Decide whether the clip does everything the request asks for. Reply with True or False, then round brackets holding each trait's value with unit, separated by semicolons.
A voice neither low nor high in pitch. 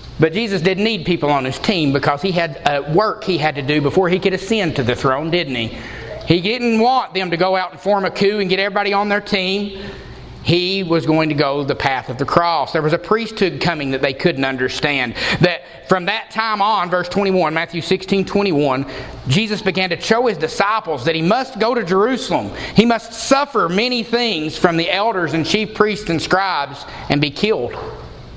True (180 Hz)